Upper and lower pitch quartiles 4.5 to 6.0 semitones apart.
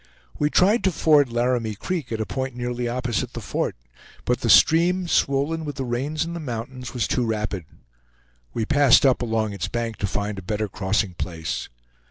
Yes: average, 4.8 semitones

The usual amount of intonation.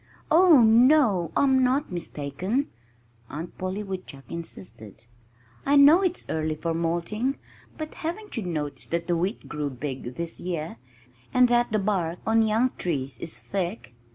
No: wide, 7.5 semitones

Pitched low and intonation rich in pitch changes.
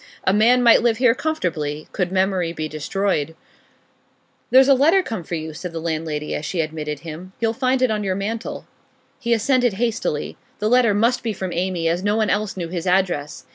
No: high, 190 Hz; wide, 5.8 semitones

